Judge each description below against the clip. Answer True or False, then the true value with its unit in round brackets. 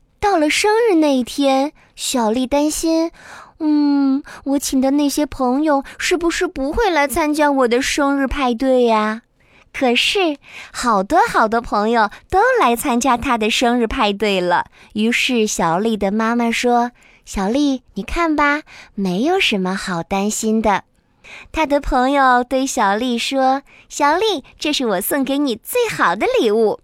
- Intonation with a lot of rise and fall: False (4.5 semitones)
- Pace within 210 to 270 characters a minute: True (215 characters per minute)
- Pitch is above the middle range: True (270 Hz)